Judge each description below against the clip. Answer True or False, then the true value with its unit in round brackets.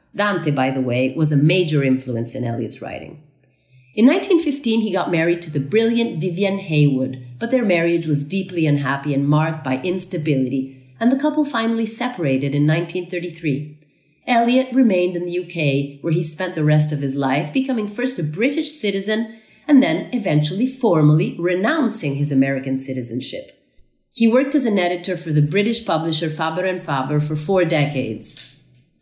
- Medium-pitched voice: True (165 Hz)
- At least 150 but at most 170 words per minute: True (160 wpm)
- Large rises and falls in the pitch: True (7.4 semitones)